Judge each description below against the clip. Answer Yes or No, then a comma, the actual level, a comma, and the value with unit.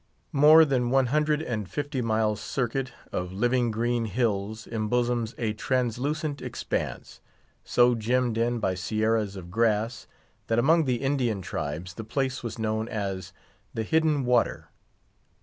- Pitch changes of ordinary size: Yes, average, 3.2 semitones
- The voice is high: No, low, 120 Hz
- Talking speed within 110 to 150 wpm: Yes, average, 140 wpm